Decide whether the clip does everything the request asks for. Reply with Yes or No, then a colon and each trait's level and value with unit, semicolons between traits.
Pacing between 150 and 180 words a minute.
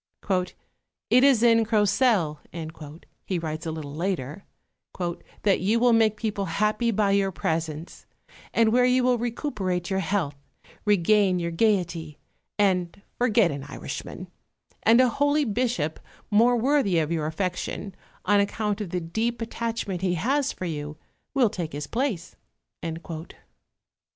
No: slow, 135 wpm